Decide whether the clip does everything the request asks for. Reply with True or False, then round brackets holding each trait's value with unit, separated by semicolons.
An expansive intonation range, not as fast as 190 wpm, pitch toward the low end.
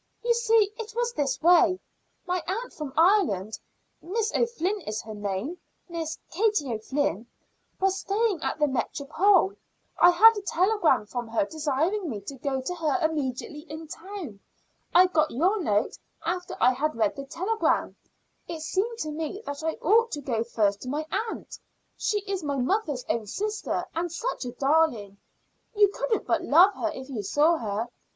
False (7.0 semitones; 170 wpm; 320 Hz)